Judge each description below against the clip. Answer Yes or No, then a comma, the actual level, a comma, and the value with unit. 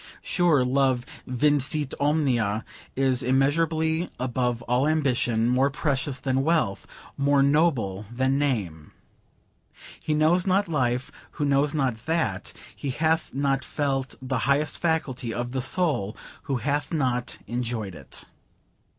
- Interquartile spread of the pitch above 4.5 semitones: No, average, 3.5 semitones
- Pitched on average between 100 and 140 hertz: Yes, low, 135 Hz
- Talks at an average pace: No, slow, 125 wpm